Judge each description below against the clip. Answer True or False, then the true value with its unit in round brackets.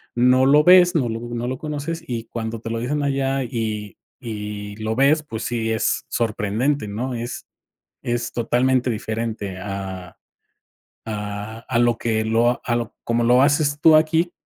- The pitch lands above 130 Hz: False (120 Hz)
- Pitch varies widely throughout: False (3.5 semitones)